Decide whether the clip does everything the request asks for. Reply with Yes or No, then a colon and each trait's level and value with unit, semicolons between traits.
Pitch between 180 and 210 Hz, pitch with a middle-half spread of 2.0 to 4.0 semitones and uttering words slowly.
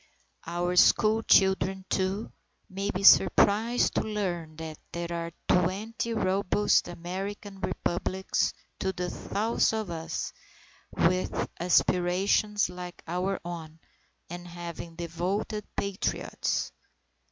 Yes: medium, 185 Hz; average, 2.7 semitones; slow, 105 wpm